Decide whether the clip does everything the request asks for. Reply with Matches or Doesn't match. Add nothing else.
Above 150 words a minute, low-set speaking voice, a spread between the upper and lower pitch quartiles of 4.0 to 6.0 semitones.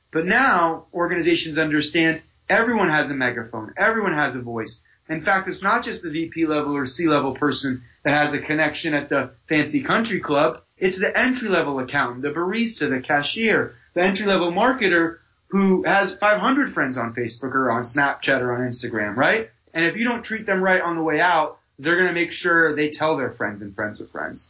Doesn't match